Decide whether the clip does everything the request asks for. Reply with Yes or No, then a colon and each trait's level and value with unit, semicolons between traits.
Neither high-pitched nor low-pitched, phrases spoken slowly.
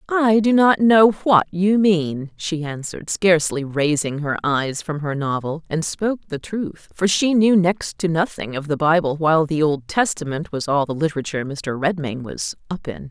No: medium, 165 Hz; average, 190 wpm